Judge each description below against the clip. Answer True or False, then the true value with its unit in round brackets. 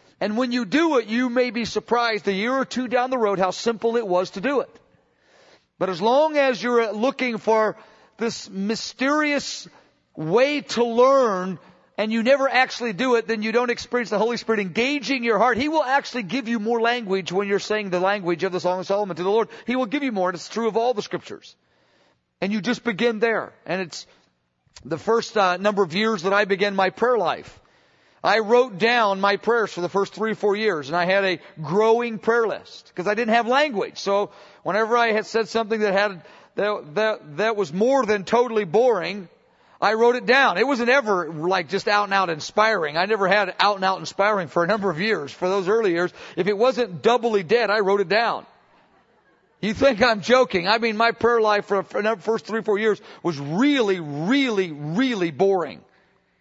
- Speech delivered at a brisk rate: True (215 wpm)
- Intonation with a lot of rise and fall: False (3.5 semitones)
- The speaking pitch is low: False (215 Hz)